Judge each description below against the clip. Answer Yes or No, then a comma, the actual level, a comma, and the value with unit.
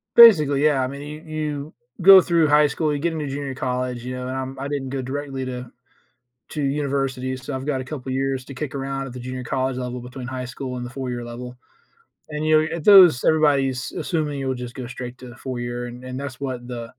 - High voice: No, low, 135 Hz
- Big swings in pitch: No, narrow, 2.5 semitones